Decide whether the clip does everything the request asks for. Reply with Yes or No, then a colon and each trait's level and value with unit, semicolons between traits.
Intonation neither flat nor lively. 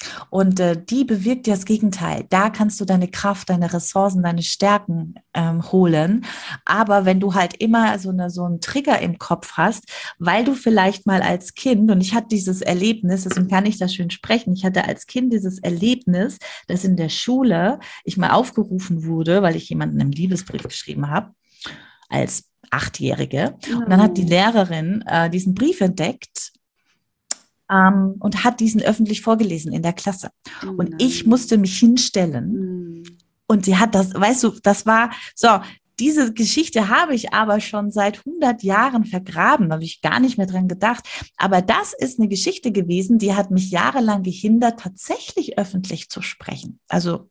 Yes: average, 3.7 semitones